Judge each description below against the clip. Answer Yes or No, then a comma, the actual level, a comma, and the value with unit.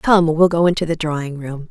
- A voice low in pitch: No, medium, 160 Hz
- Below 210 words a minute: No, fast, 245 wpm